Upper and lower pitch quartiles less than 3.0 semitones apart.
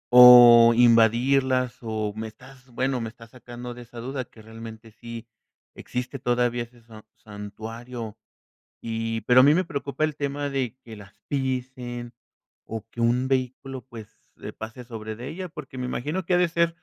Yes: narrow, 2.6 semitones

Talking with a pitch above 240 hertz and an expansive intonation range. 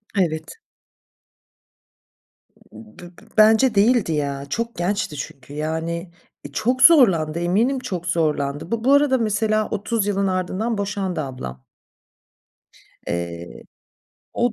No: medium, 185 Hz; wide, 6.2 semitones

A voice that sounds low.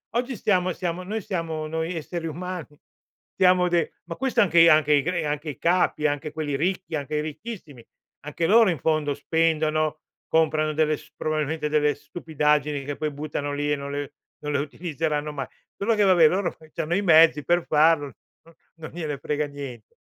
No: medium, 155 Hz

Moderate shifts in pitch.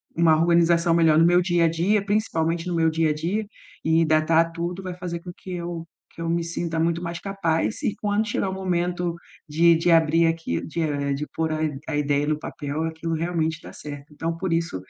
No: narrow, 1.6 semitones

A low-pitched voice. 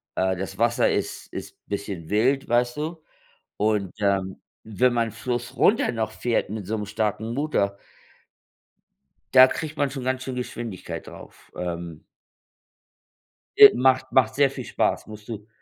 Yes: low, 115 Hz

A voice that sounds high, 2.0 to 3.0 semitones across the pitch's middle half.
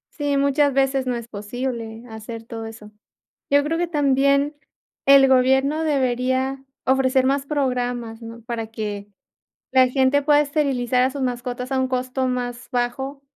Yes: very high, 260 Hz; narrow, 2.4 semitones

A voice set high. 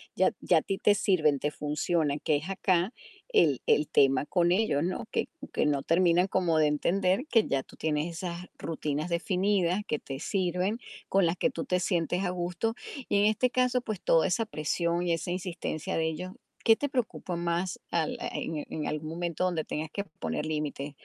No: medium, 175 Hz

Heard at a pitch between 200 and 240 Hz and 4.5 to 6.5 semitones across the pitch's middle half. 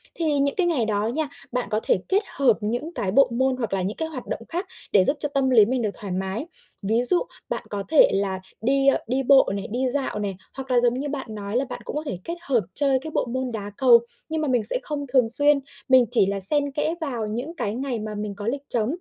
No: very high, 250 Hz; average, 4.8 semitones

